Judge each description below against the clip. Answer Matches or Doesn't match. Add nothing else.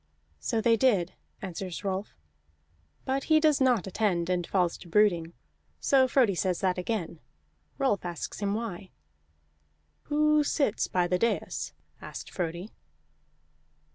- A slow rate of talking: Matches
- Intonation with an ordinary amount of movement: Doesn't match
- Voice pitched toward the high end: Matches